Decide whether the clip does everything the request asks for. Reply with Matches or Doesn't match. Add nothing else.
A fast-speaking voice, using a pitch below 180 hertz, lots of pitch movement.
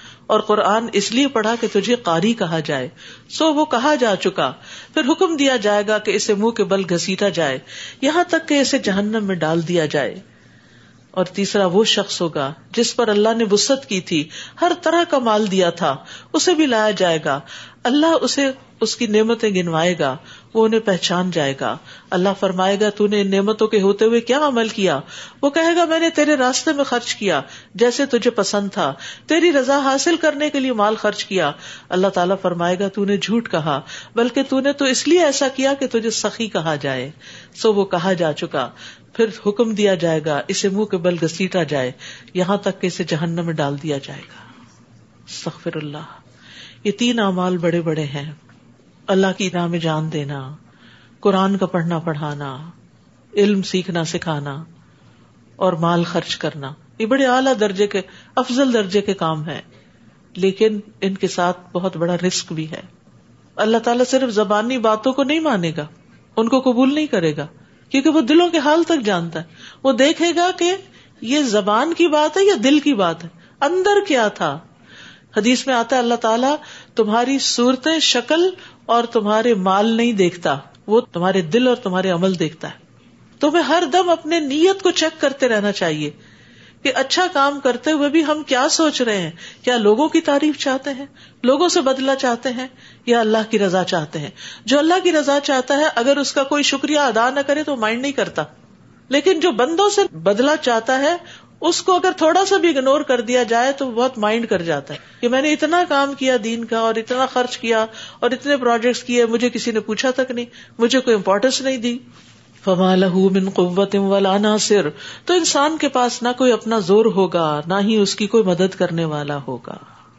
Doesn't match